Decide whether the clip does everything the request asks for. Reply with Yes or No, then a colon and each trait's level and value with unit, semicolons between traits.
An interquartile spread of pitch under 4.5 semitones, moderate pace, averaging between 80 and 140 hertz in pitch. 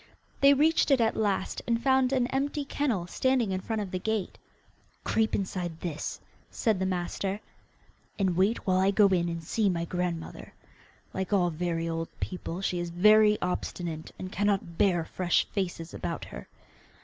No: average, 4.1 semitones; average, 170 wpm; high, 190 Hz